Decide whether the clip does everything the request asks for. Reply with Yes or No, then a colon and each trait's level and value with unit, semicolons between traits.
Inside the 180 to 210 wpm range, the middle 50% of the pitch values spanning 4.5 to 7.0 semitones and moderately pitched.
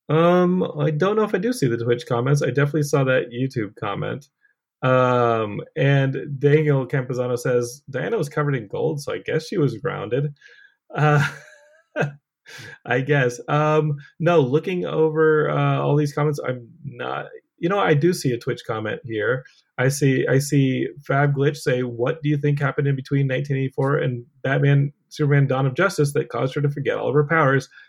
No: average, 185 wpm; average, 3.0 semitones; medium, 145 Hz